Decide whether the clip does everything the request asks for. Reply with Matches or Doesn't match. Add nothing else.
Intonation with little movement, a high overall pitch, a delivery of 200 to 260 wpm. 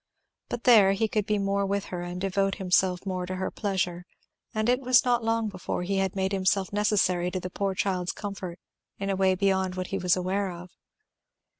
Matches